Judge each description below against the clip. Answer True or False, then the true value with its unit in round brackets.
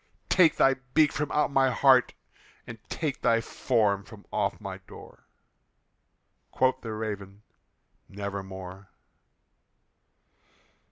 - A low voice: True (110 Hz)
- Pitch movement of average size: True (5.0 semitones)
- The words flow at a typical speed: False (105 wpm)